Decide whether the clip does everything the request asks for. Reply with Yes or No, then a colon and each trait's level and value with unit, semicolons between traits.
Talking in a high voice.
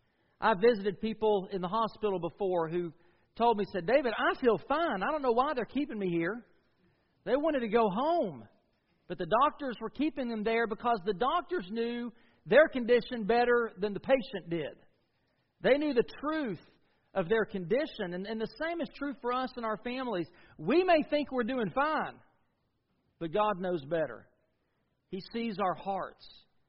Yes: high, 220 Hz